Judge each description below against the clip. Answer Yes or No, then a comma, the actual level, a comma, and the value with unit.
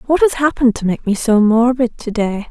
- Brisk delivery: Yes, fast, 240 wpm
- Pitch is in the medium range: No, high, 230 Hz